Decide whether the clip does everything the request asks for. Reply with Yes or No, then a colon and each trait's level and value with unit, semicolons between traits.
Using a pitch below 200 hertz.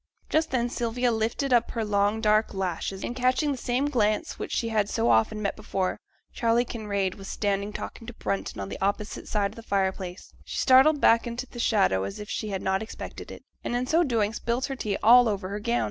No: high, 220 Hz